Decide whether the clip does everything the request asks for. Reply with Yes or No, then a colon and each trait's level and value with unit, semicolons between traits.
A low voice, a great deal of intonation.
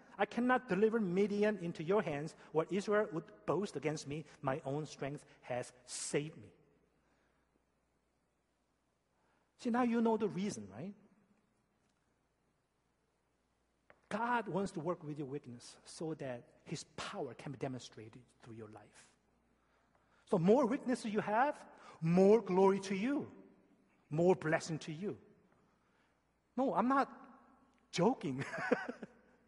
No: high, 190 Hz; wide, 7.5 semitones